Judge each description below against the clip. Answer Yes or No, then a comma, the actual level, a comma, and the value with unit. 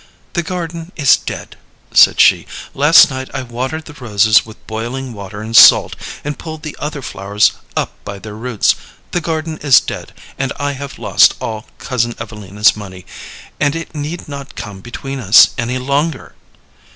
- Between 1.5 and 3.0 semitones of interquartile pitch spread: No, average, 5.3 semitones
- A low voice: Yes, low, 130 Hz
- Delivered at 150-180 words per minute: Yes, average, 170 wpm